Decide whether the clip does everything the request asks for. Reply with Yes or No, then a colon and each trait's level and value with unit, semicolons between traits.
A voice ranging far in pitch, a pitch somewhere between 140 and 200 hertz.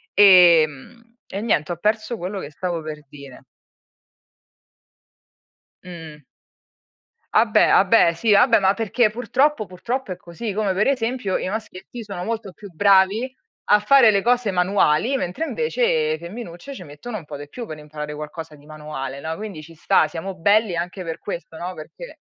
Yes: wide, 5.8 semitones; high, 190 Hz